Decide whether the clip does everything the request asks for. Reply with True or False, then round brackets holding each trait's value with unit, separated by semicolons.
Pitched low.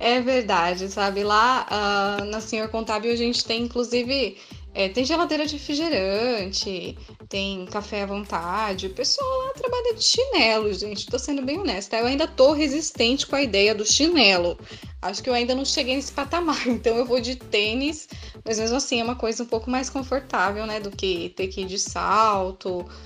False (235 Hz)